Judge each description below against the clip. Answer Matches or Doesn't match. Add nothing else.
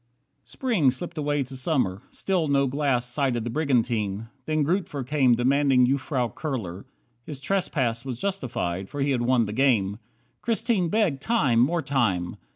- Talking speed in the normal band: Matches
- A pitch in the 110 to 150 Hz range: Matches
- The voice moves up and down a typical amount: Matches